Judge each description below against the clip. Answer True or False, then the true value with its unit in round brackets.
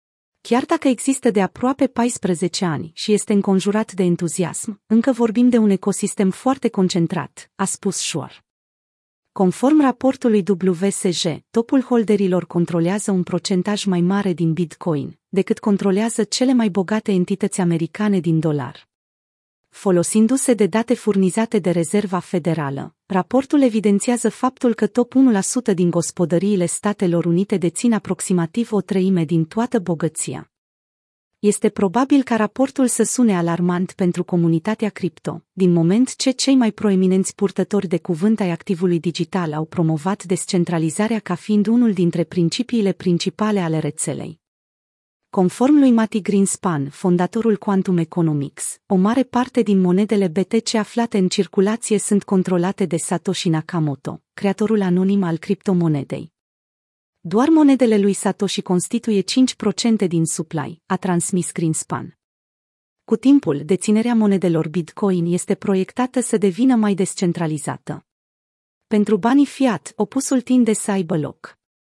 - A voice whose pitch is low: False (195 Hz)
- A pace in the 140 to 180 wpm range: False (130 wpm)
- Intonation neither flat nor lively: True (4.1 semitones)